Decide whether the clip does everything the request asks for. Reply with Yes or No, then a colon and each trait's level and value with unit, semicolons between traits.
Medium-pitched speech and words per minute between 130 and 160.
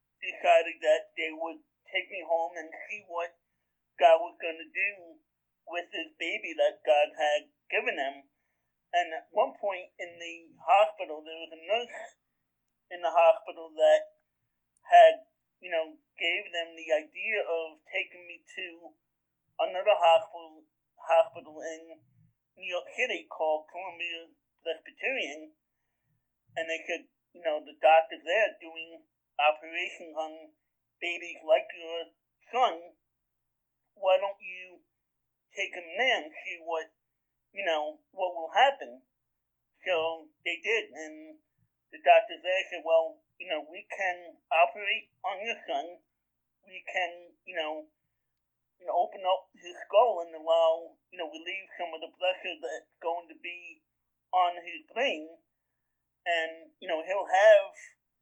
Yes: medium, 165 Hz; average, 140 wpm